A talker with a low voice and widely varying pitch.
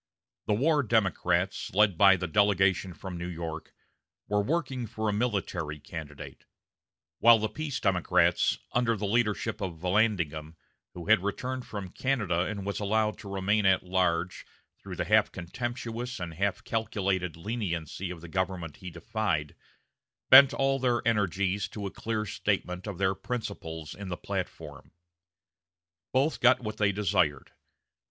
No: low, 100 Hz; average, 3.8 semitones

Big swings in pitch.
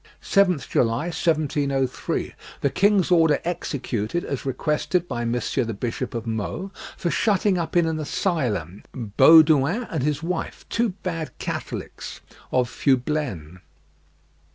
Yes: wide, 5.9 semitones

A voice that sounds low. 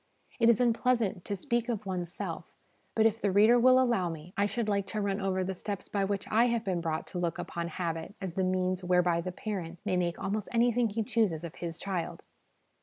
No: high, 195 Hz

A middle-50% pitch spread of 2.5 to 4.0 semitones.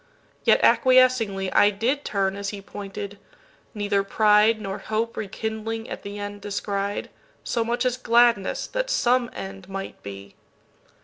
Yes: average, 2.9 semitones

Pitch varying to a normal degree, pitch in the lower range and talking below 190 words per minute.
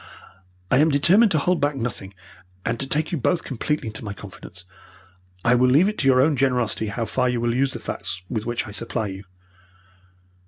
No: average, 4.7 semitones; low, 125 Hz; fast, 205 wpm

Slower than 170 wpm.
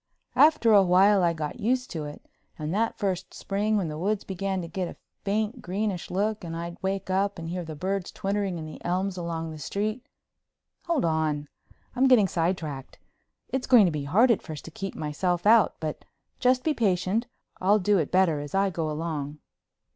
No: average, 190 wpm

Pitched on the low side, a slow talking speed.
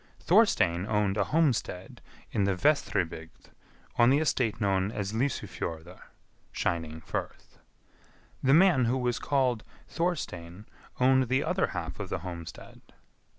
Yes: low, 110 Hz; slow, 125 wpm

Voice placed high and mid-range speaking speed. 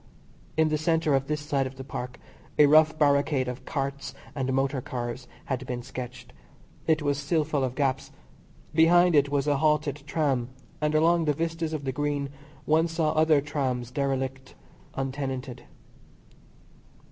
No: medium, 140 Hz; average, 160 wpm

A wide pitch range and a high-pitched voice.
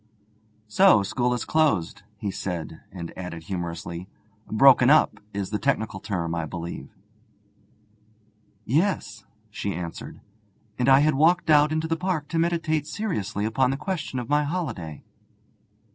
No: wide, 8.8 semitones; low, 120 Hz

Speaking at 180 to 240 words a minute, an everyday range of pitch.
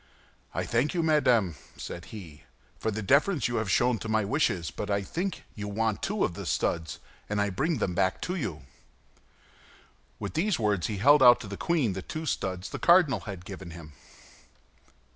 No: average, 190 wpm; wide, 7.2 semitones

